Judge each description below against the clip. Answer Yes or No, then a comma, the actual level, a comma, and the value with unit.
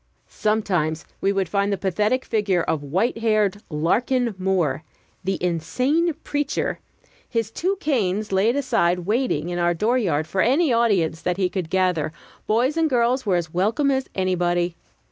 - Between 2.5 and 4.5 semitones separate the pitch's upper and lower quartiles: No, wide, 5.4 semitones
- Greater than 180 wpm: No, average, 155 wpm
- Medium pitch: No, high, 200 Hz